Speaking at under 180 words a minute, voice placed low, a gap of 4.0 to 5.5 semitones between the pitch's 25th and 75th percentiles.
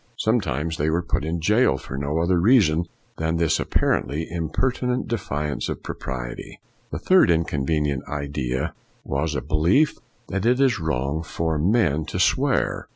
Yes: average, 155 wpm; very low, 80 Hz; average, 4.8 semitones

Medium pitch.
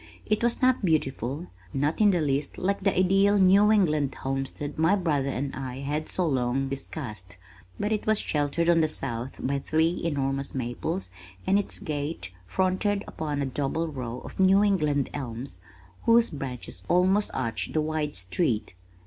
Yes: medium, 150 Hz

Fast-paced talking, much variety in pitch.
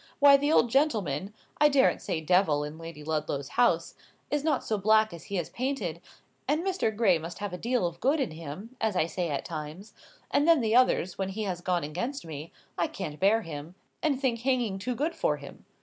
Yes: fast, 215 wpm; wide, 7.5 semitones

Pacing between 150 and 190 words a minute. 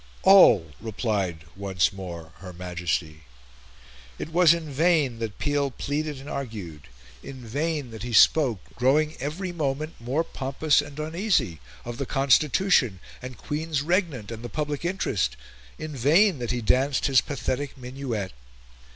No: average, 140 wpm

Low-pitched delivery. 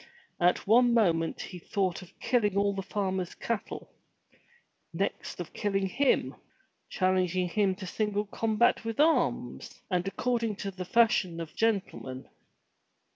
No: high, 195 Hz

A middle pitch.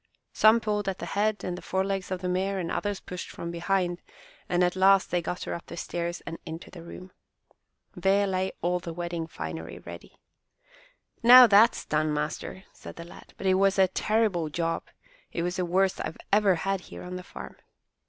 Yes: medium, 180 Hz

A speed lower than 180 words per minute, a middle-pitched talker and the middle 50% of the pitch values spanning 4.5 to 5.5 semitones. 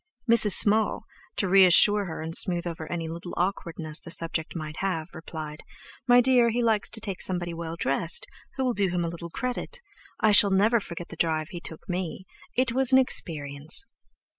No: average, 190 wpm; medium, 180 Hz; average, 4.8 semitones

